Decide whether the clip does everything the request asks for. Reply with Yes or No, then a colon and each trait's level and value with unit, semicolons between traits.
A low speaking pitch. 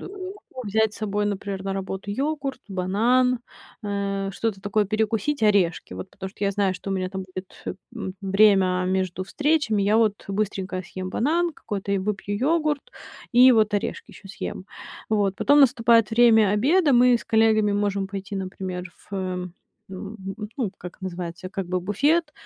No: high, 205 Hz